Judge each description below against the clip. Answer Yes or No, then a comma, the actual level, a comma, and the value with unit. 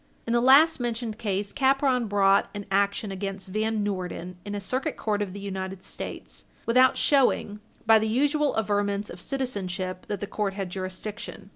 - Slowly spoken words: No, average, 170 wpm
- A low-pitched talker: No, high, 205 Hz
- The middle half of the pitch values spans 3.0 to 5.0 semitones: Yes, average, 3.4 semitones